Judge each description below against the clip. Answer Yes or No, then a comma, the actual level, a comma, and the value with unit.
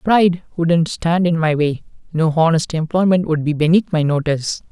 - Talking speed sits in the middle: Yes, average, 180 wpm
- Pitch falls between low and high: Yes, medium, 165 Hz